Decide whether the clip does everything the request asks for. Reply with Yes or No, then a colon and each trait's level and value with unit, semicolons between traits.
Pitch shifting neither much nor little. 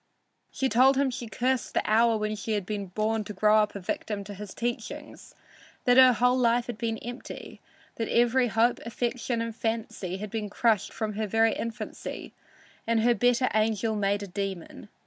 No: narrow, 2.3 semitones